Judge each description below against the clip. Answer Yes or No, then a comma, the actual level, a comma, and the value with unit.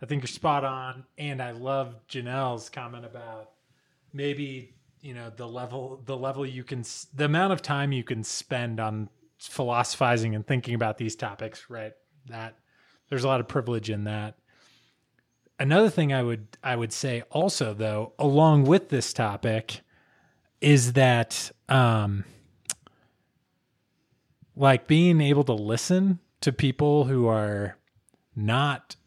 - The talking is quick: No, average, 140 wpm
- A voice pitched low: Yes, low, 130 Hz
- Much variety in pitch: No, average, 3.8 semitones